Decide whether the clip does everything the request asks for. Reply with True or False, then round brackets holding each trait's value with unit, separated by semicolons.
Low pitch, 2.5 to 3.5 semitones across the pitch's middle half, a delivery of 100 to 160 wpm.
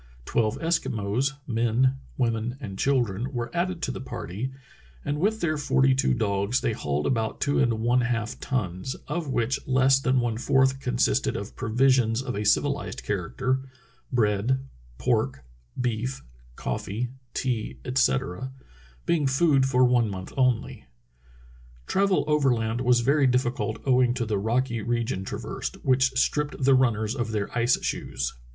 True (125 Hz; 3.1 semitones; 155 wpm)